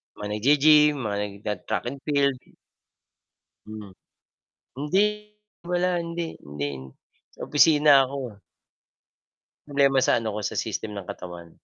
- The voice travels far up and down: Yes, wide, 6.4 semitones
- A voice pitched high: No, low, 135 Hz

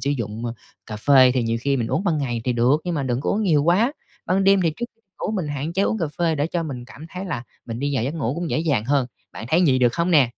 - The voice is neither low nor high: Yes, medium, 145 Hz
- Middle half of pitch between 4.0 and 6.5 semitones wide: Yes, wide, 5.5 semitones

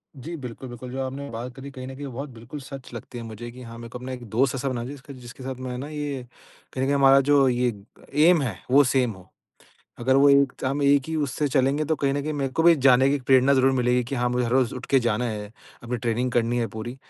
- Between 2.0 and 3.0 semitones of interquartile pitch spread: Yes, narrow, 2.4 semitones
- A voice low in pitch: Yes, low, 130 Hz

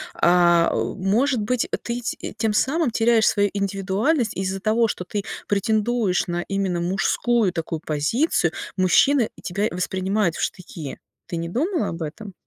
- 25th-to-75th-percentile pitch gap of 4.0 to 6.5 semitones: Yes, average, 4.4 semitones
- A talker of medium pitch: No, high, 200 Hz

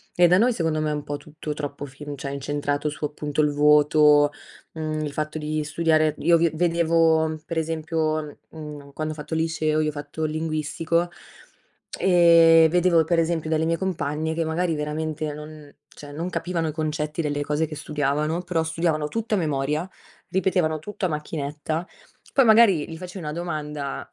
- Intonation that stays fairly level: Yes, narrow, 1.8 semitones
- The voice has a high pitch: No, medium, 155 Hz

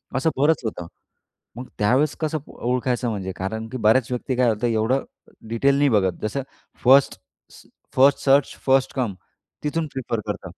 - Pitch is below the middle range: Yes, low, 125 Hz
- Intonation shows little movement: No, average, 3.6 semitones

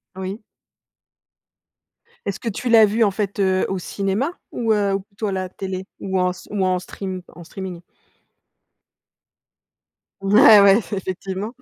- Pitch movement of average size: No, narrow, 1.9 semitones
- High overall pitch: Yes, high, 195 Hz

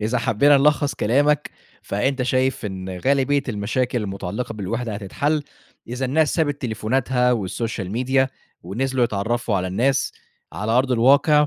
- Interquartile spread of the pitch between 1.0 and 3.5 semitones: No, average, 4.1 semitones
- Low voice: Yes, low, 125 Hz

